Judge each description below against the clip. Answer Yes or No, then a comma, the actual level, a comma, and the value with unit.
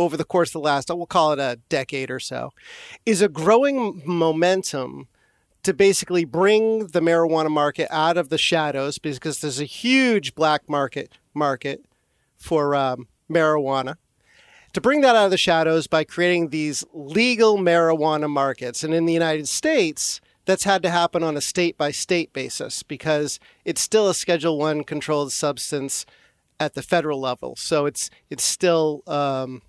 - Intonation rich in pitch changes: No, average, 3.4 semitones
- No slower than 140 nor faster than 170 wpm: Yes, average, 160 wpm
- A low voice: No, medium, 160 Hz